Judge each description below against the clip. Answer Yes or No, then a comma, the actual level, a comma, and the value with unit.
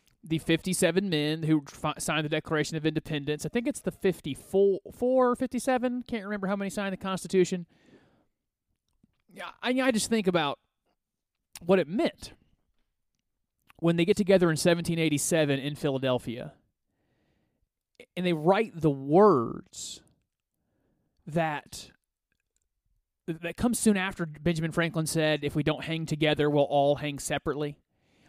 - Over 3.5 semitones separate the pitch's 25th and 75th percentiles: Yes, average, 4.3 semitones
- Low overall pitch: No, medium, 165 Hz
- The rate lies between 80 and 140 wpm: Yes, slow, 135 wpm